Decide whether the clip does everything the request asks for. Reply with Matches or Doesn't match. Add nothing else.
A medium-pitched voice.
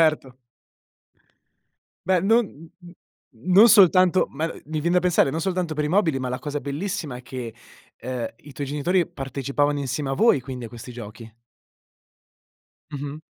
Matches